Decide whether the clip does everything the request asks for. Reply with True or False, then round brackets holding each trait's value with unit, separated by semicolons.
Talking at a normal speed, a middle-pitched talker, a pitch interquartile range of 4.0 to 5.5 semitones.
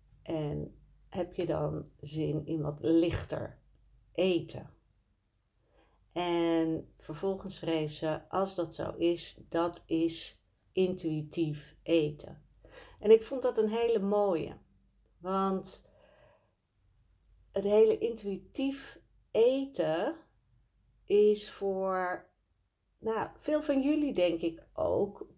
False (100 wpm; 170 Hz; 4.7 semitones)